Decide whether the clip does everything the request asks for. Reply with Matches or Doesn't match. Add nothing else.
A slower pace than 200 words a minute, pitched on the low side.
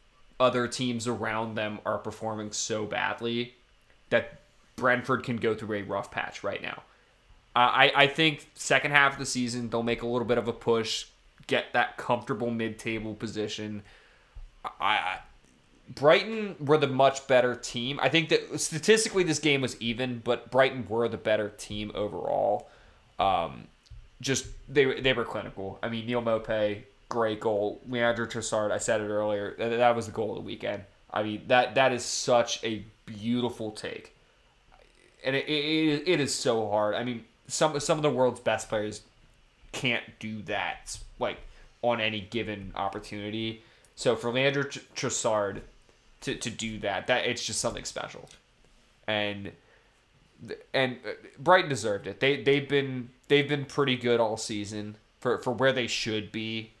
Matches